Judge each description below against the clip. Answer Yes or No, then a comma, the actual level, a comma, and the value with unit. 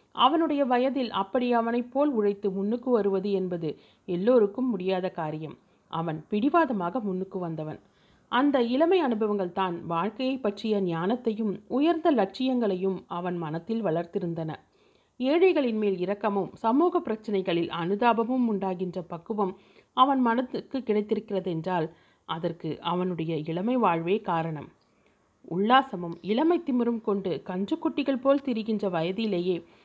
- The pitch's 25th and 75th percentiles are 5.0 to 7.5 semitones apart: Yes, wide, 5.6 semitones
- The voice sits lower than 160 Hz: No, high, 205 Hz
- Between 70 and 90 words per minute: No, average, 105 wpm